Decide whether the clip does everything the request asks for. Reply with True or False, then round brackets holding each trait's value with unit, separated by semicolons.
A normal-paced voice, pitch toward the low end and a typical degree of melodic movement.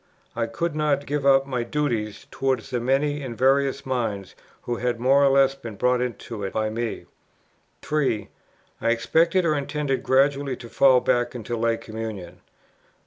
True (170 wpm; 130 Hz; 3.2 semitones)